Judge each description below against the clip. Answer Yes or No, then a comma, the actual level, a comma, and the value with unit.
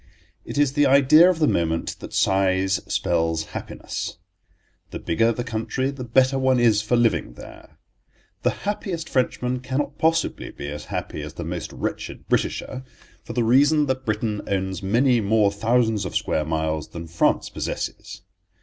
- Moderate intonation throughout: No, wide, 5.7 semitones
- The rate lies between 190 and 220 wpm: No, average, 160 wpm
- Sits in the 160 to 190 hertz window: No, low, 115 Hz